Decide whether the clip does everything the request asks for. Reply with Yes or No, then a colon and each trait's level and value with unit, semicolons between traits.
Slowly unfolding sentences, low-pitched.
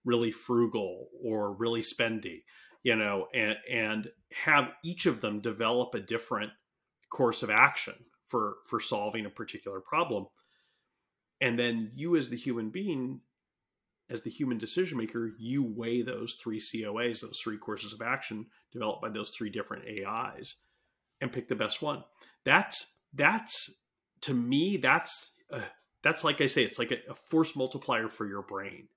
No: average, 160 wpm; low, 115 Hz